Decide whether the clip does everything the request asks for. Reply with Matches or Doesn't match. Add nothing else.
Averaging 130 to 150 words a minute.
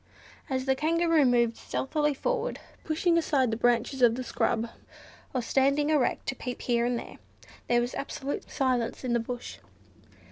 Doesn't match